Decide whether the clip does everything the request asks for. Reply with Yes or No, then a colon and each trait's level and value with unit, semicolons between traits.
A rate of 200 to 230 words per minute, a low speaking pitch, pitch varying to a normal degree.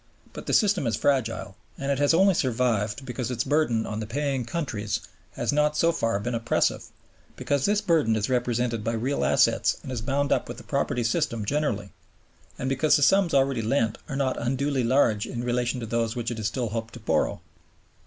Yes: fast, 205 wpm; low, 125 Hz; average, 3.8 semitones